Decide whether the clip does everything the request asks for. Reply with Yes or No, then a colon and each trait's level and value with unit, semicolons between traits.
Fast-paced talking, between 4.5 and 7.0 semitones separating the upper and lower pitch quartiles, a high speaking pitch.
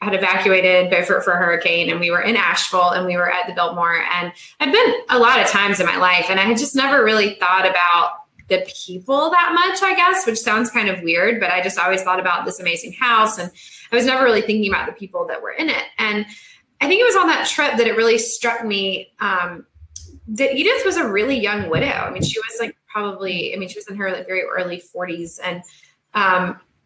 Yes: fast, 240 wpm; average, 5.2 semitones; high, 195 Hz